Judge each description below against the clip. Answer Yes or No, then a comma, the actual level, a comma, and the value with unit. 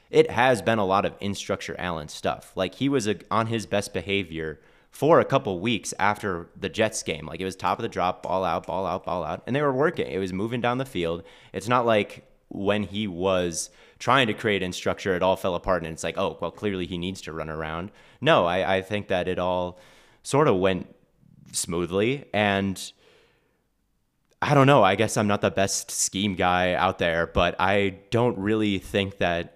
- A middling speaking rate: No, fast, 210 wpm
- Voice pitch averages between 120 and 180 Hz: No, very low, 95 Hz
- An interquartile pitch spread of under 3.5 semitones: Yes, average, 2.7 semitones